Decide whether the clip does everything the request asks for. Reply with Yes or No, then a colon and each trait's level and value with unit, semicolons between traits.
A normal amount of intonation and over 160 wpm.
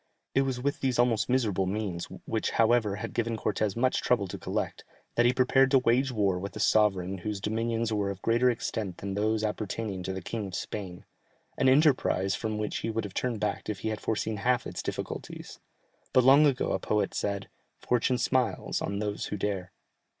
Yes: average, 3.6 semitones; average, 200 wpm